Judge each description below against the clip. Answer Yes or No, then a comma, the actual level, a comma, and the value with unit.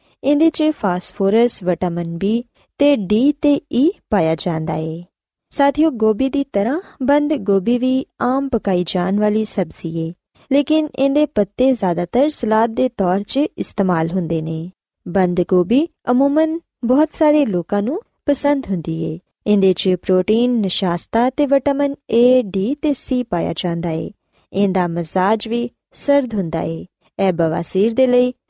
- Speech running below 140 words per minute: No, average, 145 wpm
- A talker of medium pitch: No, high, 220 Hz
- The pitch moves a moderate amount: No, wide, 7.4 semitones